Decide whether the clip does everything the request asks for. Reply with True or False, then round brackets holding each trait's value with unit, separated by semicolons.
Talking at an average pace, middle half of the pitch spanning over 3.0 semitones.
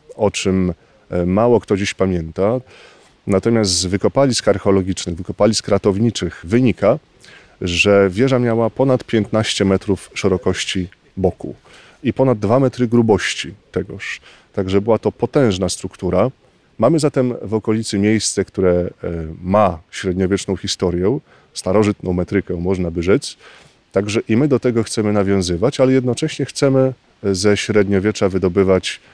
True (125 wpm; 3.5 semitones)